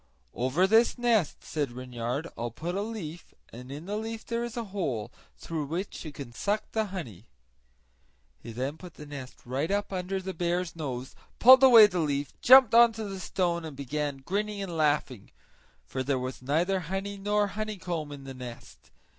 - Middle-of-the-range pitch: Yes, medium, 170 Hz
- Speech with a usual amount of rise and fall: No, wide, 6.8 semitones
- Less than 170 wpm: No, average, 185 wpm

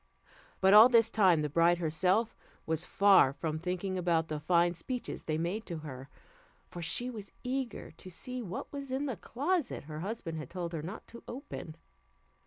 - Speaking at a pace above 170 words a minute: Yes, average, 185 wpm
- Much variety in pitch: Yes, wide, 6.1 semitones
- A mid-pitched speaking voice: Yes, medium, 180 Hz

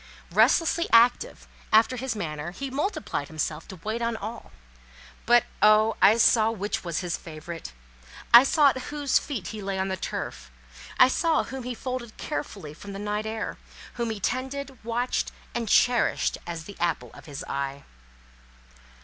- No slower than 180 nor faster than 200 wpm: No, average, 165 wpm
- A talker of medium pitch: No, high, 220 Hz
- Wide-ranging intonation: Yes, wide, 5.7 semitones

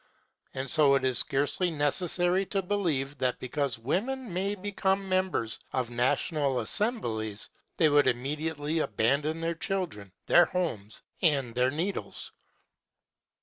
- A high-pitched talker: No, medium, 150 Hz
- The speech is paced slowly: Yes, slow, 125 wpm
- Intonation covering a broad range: Yes, wide, 6.0 semitones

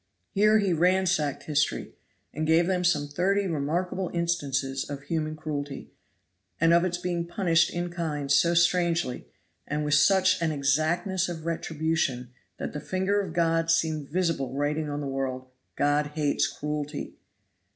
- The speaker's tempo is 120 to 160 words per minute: Yes, average, 150 wpm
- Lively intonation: No, average, 3.2 semitones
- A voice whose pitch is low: No, medium, 160 Hz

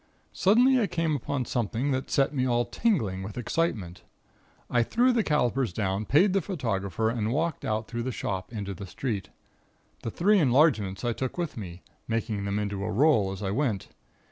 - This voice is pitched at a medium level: No, low, 120 Hz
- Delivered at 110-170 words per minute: No, average, 185 wpm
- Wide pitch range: Yes, wide, 6.9 semitones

